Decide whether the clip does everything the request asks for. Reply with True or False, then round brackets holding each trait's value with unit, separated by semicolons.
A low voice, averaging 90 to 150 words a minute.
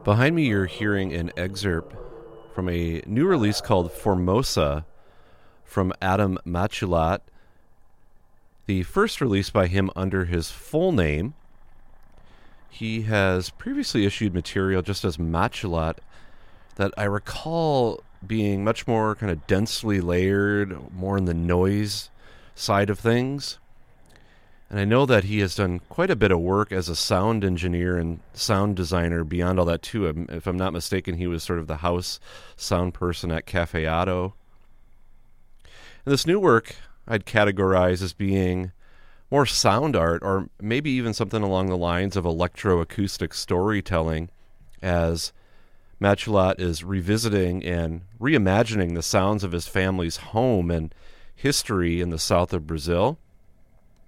True (95 Hz; 140 wpm)